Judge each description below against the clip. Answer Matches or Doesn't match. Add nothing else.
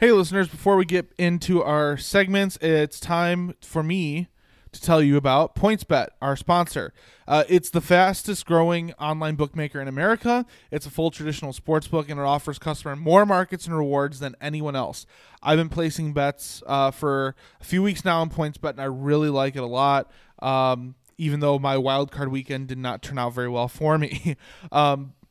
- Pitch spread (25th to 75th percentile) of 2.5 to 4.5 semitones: Matches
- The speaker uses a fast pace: Doesn't match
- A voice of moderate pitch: Matches